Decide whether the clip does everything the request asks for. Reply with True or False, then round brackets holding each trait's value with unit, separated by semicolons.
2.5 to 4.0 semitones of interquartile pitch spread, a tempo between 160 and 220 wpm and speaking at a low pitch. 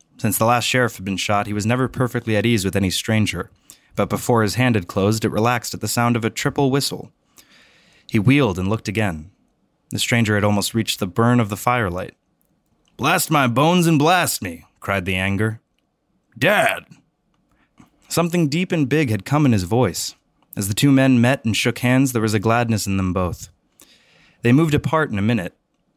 True (3.6 semitones; 200 wpm; 115 Hz)